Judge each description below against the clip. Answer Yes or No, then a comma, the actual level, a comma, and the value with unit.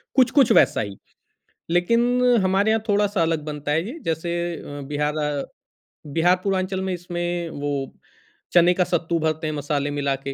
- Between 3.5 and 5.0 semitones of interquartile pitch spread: Yes, average, 4.5 semitones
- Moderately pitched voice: Yes, medium, 175 Hz